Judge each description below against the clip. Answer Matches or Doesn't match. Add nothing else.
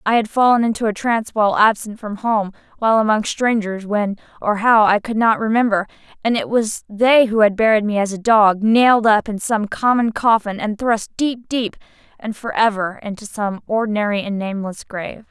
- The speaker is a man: Doesn't match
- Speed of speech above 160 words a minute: Matches